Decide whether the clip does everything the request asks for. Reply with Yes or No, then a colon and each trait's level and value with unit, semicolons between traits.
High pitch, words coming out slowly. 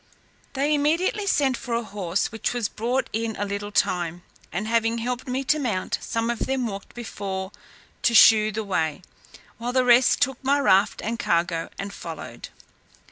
No: high, 230 Hz; average, 175 wpm